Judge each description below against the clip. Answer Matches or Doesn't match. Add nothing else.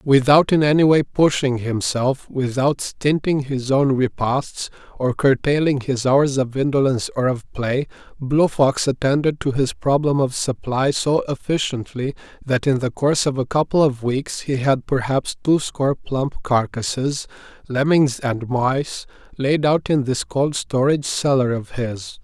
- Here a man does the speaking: Matches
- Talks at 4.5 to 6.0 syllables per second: Doesn't match